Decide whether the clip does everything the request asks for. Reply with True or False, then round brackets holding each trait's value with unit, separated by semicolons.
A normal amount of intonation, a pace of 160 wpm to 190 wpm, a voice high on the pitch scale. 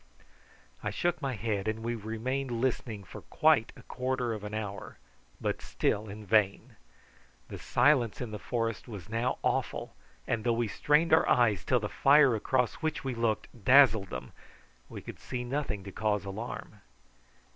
False (3.4 semitones; 165 wpm; 115 Hz)